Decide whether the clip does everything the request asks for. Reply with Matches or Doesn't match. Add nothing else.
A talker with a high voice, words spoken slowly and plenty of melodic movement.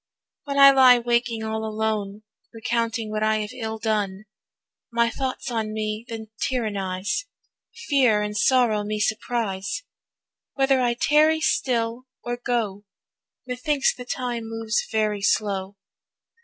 Doesn't match